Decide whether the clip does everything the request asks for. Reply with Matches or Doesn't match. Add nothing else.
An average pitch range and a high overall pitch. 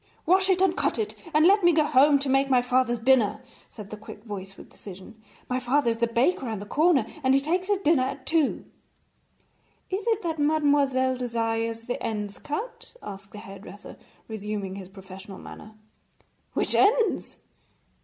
Doesn't match